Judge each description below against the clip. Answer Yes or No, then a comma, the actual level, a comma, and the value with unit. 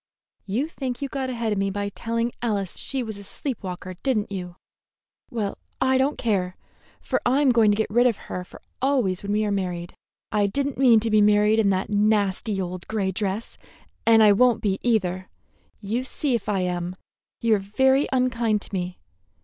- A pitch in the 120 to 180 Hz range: No, high, 215 Hz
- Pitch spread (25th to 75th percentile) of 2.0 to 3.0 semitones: No, average, 3.8 semitones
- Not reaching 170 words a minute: No, average, 200 wpm